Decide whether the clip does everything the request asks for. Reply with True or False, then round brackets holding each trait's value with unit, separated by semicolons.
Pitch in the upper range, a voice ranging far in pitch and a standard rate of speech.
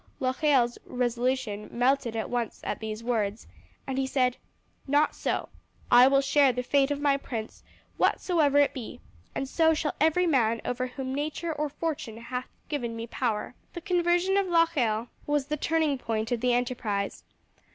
False (260 Hz; 3.8 semitones; 165 wpm)